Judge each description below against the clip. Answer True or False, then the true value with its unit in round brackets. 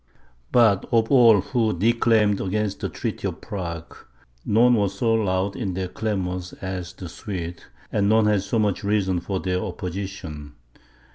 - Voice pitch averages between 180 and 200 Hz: False (100 Hz)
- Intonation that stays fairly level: False (3.0 semitones)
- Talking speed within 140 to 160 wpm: True (155 wpm)